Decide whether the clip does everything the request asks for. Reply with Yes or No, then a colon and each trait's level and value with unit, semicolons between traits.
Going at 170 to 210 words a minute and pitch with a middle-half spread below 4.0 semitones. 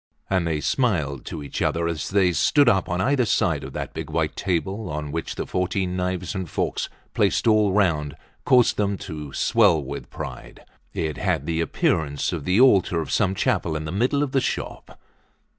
No: average, 190 wpm; average, 4.8 semitones